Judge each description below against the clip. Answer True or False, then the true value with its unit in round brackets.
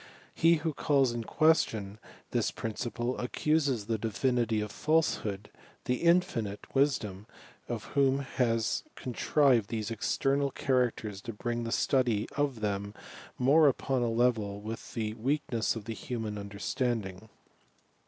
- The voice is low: True (120 Hz)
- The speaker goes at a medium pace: False (130 wpm)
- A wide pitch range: False (4.1 semitones)